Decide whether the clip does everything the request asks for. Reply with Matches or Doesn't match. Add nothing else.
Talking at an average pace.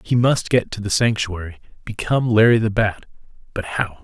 Matches